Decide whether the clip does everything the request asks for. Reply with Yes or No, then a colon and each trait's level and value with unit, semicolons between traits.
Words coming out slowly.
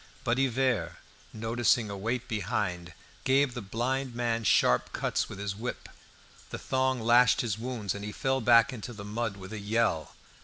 No: average, 170 wpm